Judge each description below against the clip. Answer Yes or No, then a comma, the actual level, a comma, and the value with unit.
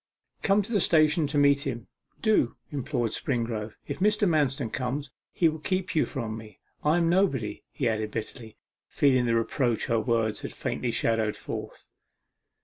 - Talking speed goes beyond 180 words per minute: No, average, 165 wpm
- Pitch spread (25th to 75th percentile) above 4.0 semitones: Yes, wide, 5.6 semitones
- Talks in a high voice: No, low, 130 Hz